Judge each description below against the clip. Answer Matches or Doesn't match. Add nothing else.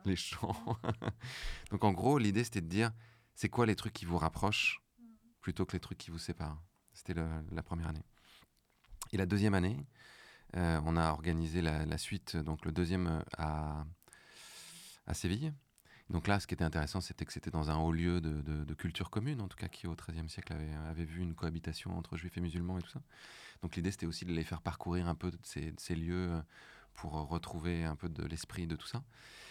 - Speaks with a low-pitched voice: Matches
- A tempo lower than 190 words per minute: Doesn't match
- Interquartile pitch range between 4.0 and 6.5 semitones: Doesn't match